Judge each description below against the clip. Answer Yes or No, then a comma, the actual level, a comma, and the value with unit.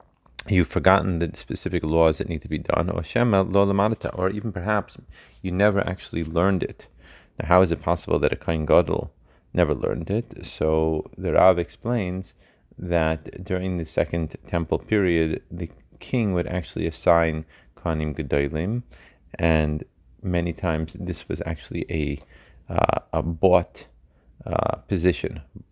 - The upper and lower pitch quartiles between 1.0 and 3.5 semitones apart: Yes, average, 2.9 semitones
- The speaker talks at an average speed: Yes, average, 140 wpm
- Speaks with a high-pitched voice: No, very low, 85 Hz